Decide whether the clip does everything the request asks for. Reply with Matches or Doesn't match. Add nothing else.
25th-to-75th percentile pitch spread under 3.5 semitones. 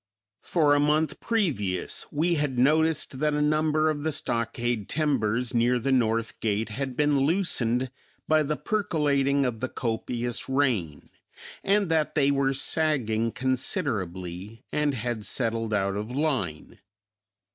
Doesn't match